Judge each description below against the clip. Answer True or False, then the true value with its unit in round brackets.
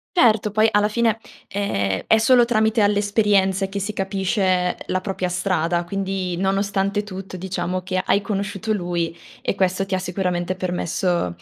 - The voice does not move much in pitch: True (2.2 semitones)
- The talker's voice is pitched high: True (195 Hz)